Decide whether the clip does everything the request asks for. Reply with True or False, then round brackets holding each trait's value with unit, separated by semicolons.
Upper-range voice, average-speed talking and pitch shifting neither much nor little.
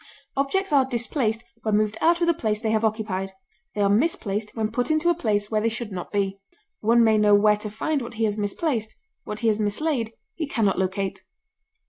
False (220 Hz; 215 wpm; 3.0 semitones)